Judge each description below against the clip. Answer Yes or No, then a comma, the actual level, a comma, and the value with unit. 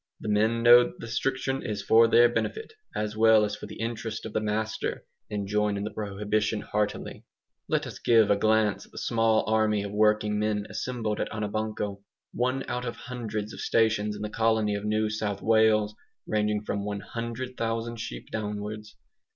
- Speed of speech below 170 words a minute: No, average, 180 wpm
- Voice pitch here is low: Yes, low, 110 Hz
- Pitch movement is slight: Yes, narrow, 1.4 semitones